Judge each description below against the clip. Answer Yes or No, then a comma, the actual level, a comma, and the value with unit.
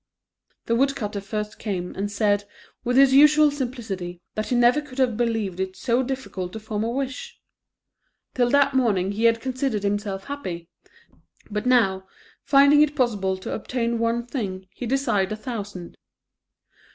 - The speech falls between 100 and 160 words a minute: Yes, average, 155 wpm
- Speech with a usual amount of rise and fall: Yes, average, 4.5 semitones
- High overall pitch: Yes, high, 230 Hz